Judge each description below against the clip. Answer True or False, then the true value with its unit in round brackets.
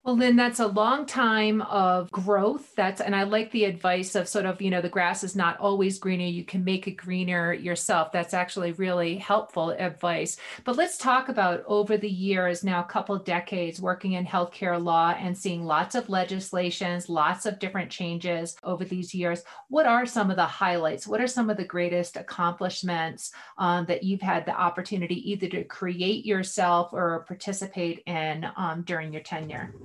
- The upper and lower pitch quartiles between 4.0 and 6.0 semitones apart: False (2.6 semitones)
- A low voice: False (185 Hz)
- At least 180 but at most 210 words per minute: True (190 wpm)